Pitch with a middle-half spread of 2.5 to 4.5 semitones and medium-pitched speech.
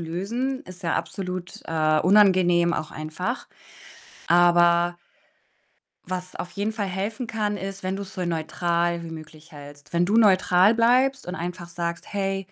Yes: average, 2.8 semitones; medium, 180 Hz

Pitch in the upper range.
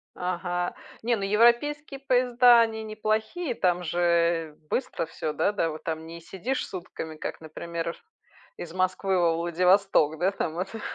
No: medium, 180 Hz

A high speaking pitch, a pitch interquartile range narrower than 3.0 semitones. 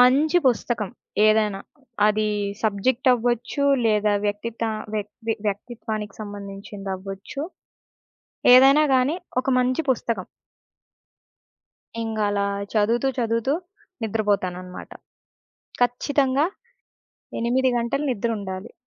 No: high, 225 Hz; average, 3.5 semitones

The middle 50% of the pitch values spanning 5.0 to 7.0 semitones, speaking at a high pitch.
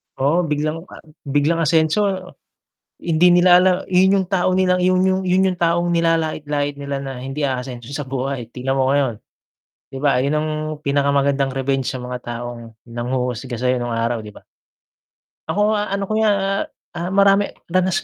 No: wide, 5.6 semitones; medium, 145 Hz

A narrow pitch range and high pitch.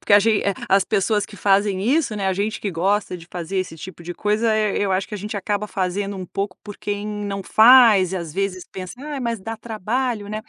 Yes: narrow, 2.2 semitones; high, 205 Hz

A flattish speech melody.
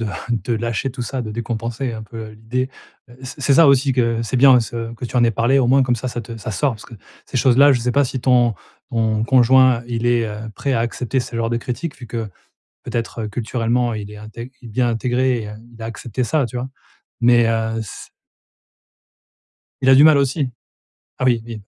Yes: narrow, 2.2 semitones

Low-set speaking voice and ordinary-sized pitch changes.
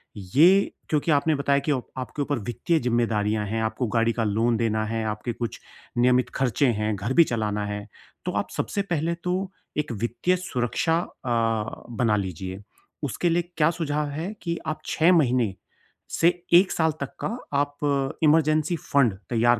No: low, 125 Hz; wide, 5.9 semitones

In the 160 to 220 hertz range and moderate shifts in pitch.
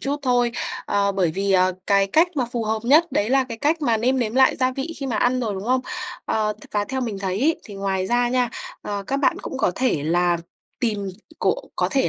No: high, 235 Hz; average, 4.7 semitones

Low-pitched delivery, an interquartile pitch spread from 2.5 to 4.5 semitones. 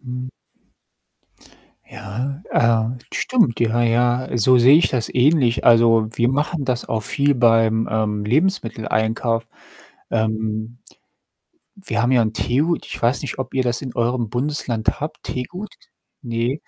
Yes: low, 120 Hz; average, 2.8 semitones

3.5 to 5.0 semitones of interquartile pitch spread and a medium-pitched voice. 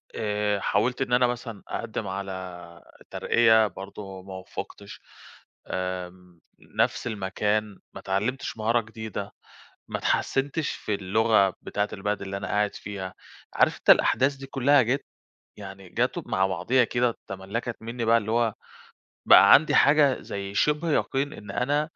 No: average, 4.0 semitones; low, 105 Hz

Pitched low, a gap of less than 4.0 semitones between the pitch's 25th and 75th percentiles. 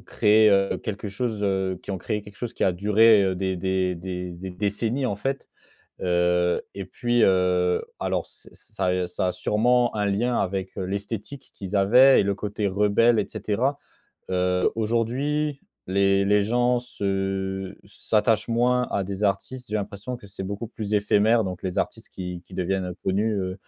Yes: low, 100 Hz; average, 3.1 semitones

